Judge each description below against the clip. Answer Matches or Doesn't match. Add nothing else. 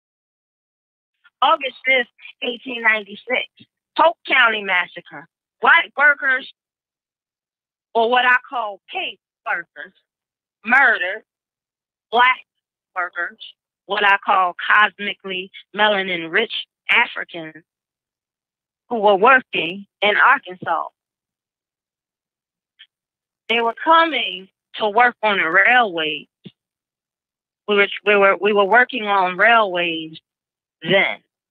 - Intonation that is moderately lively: Matches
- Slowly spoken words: Matches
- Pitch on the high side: Matches